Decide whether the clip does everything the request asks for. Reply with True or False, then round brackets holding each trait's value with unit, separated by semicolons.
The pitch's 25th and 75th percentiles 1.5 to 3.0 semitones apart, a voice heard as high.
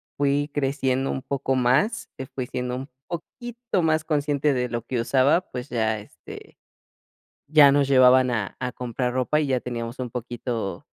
False (2.7 semitones; 130 Hz)